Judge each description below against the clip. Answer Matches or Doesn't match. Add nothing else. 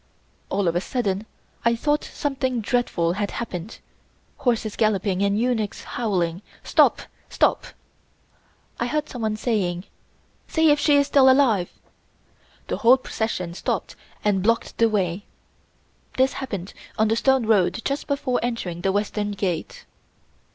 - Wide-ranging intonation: Doesn't match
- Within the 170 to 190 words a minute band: Doesn't match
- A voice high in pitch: Matches